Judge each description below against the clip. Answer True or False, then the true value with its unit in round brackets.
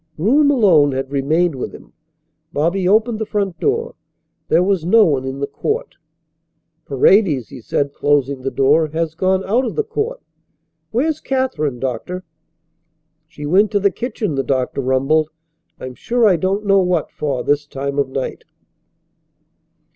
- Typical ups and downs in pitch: False (7.2 semitones)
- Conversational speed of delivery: True (155 wpm)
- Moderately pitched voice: True (165 Hz)